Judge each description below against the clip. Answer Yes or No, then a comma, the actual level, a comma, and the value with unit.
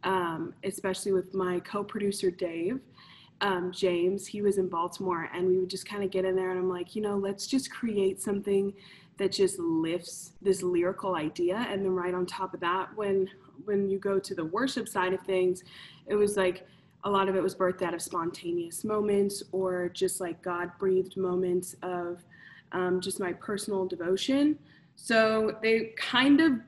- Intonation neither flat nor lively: No, narrow, 1.9 semitones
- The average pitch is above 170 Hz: Yes, medium, 185 Hz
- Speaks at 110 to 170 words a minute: No, average, 185 wpm